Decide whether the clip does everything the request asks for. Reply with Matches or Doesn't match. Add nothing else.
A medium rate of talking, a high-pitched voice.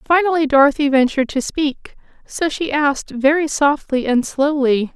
Matches